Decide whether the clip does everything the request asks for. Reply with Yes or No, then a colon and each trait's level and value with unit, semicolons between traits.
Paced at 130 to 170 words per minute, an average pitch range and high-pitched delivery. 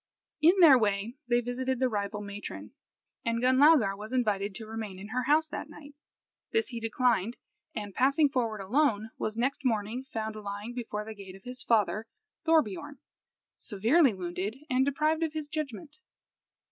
Yes: average, 160 wpm; average, 4.7 semitones; high, 235 Hz